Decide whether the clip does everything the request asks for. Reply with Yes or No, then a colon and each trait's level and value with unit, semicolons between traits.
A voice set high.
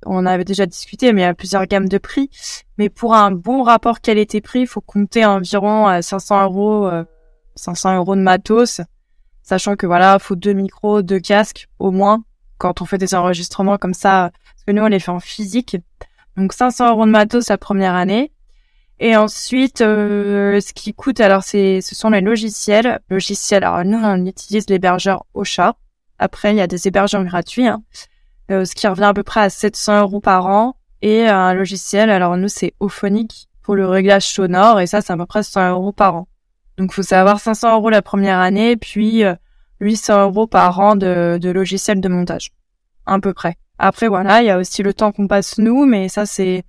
Yes: high, 200 Hz